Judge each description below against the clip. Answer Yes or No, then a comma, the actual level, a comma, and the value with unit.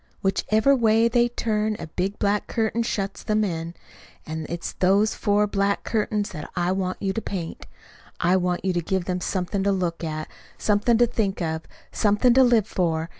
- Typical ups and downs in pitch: Yes, average, 3.4 semitones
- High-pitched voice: Yes, high, 195 Hz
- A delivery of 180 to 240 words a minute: Yes, average, 185 wpm